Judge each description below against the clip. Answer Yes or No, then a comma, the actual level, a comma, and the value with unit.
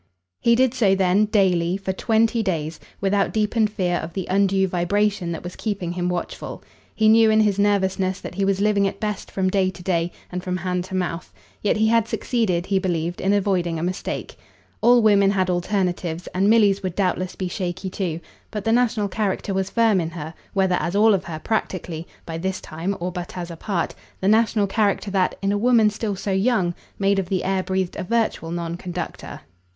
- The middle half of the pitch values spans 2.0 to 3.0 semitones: Yes, average, 2.7 semitones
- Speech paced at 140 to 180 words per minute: No, fast, 205 wpm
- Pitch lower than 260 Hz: Yes, high, 190 Hz